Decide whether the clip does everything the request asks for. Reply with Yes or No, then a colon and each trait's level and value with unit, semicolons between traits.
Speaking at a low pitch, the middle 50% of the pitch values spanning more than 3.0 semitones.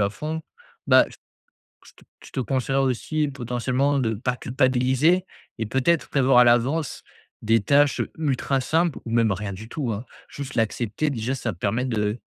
Yes: low, 125 Hz; average, 3.7 semitones